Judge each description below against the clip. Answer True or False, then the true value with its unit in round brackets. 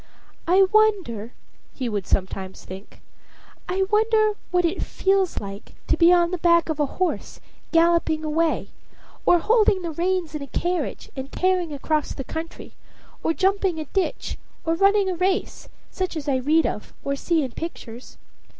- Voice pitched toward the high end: True (335 Hz)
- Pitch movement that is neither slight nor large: True (4.4 semitones)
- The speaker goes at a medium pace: True (165 wpm)